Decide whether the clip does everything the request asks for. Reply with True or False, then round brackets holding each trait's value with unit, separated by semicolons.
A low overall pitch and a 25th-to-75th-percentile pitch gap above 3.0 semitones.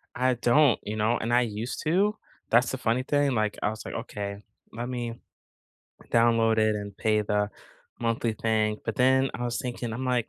False (115 Hz; 2.5 semitones)